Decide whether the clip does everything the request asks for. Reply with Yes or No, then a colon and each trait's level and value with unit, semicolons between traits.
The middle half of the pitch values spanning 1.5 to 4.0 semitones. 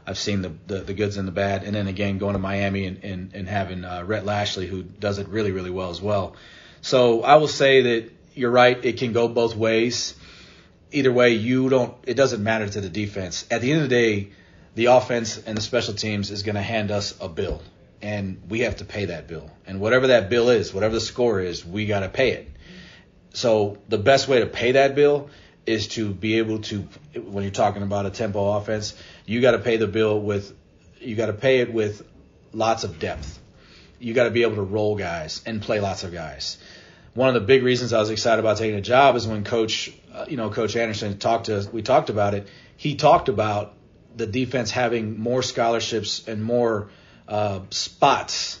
Yes: average, 2.8 semitones